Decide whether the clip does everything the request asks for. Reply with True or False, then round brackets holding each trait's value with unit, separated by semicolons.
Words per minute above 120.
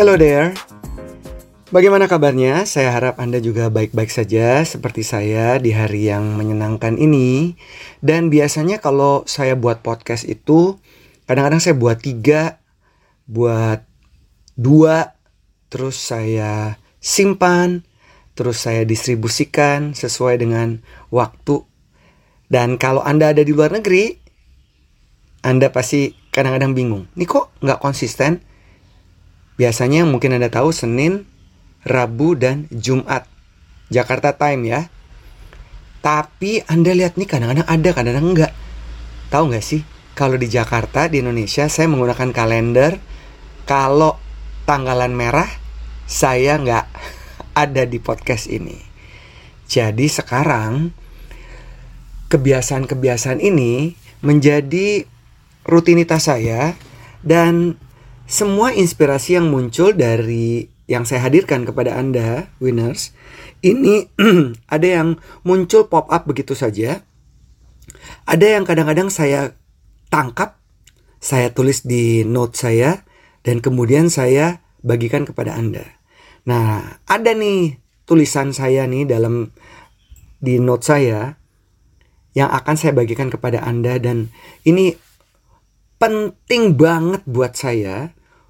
False (110 wpm)